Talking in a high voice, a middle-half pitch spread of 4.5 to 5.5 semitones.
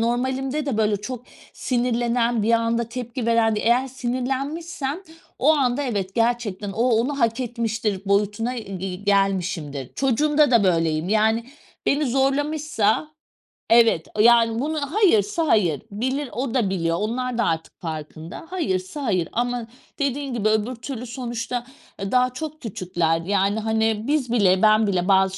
No: high, 230 Hz; average, 4.1 semitones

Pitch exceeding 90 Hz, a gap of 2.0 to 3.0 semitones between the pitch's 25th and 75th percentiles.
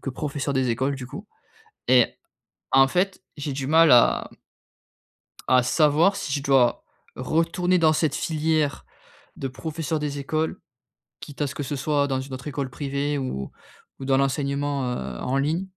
Yes: medium, 140 Hz; average, 2.7 semitones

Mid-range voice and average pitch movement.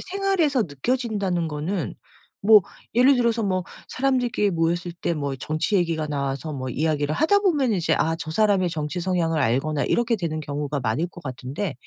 No: medium, 170 Hz; wide, 6.9 semitones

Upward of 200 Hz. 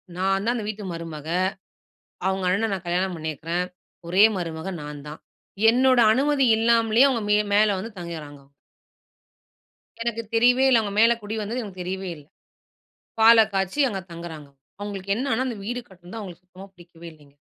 No: high, 195 Hz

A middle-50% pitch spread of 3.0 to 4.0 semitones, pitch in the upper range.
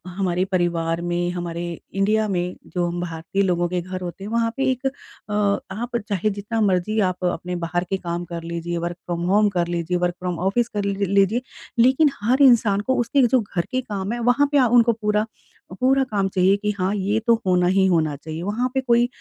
No: average, 4.4 semitones; high, 195 Hz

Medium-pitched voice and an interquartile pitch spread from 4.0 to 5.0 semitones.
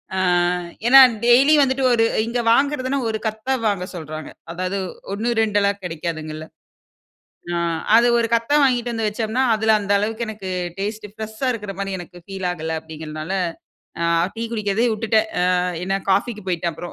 No: high, 210 Hz; average, 4.3 semitones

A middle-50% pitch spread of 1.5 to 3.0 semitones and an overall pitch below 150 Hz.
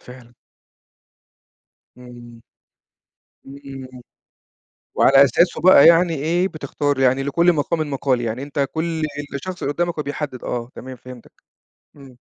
No: average, 3.8 semitones; medium, 140 Hz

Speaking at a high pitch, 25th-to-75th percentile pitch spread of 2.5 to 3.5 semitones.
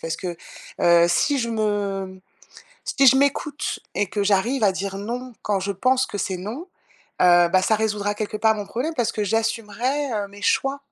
No: high, 210 Hz; average, 4.2 semitones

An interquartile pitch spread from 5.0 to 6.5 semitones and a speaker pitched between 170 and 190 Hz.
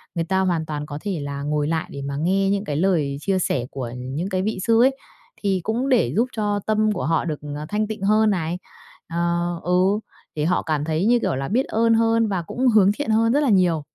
Yes: wide, 5.5 semitones; medium, 185 Hz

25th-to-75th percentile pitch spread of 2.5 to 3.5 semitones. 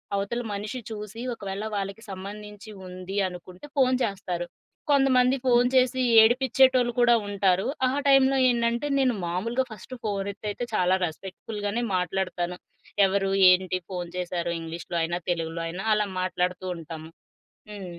No: average, 4.7 semitones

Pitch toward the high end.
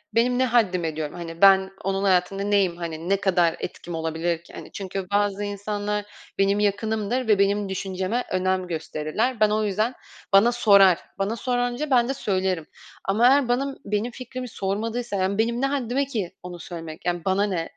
Yes: high, 200 Hz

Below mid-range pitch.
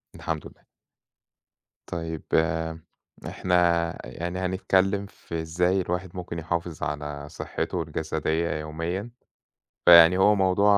Yes: very low, 85 Hz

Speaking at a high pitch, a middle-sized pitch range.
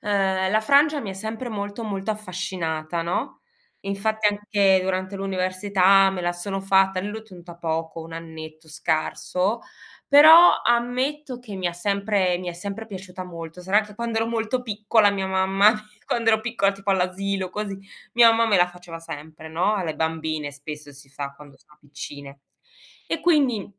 Yes: high, 195 Hz; average, 3.8 semitones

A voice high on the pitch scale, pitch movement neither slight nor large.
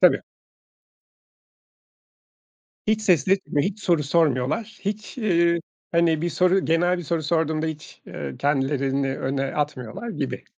No: medium, 165 Hz; average, 4.3 semitones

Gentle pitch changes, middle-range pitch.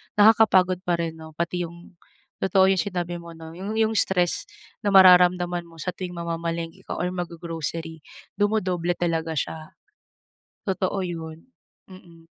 Yes: narrow, 2.0 semitones; medium, 175 Hz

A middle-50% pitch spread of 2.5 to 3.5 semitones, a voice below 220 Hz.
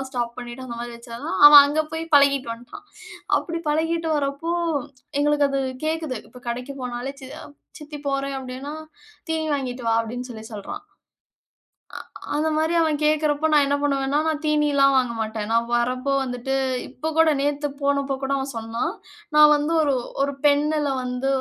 No: average, 3.2 semitones; very high, 280 Hz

